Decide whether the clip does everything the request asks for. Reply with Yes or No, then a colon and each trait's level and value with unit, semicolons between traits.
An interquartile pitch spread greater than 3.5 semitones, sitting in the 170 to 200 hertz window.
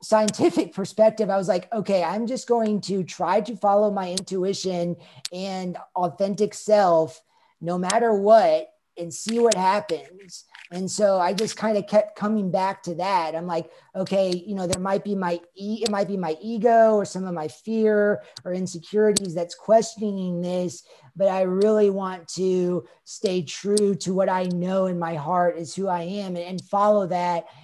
No: average, 3.0 semitones; high, 190 Hz